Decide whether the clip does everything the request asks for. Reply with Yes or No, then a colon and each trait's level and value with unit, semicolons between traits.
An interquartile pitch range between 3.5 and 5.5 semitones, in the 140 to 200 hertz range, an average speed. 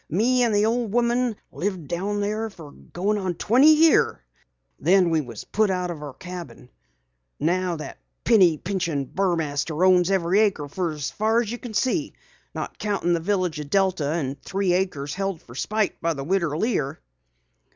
Yes: average, 4.5 semitones; medium, 185 Hz; average, 170 wpm